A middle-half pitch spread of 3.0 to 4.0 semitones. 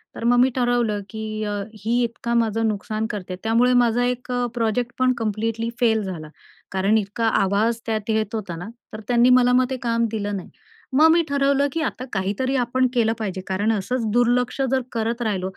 No: narrow, 2.5 semitones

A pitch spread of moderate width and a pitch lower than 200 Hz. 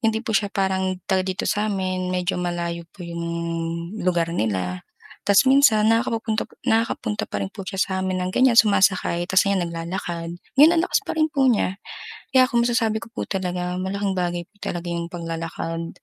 Yes: average, 3.9 semitones; medium, 185 Hz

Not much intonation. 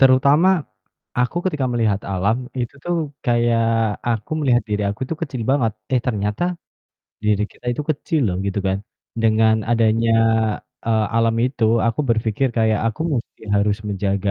No: average, 3.3 semitones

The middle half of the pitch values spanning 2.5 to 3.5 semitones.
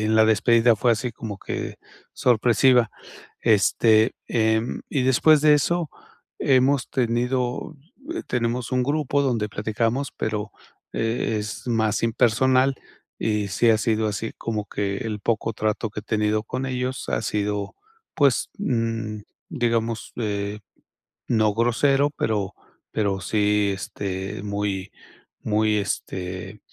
Yes: average, 3.0 semitones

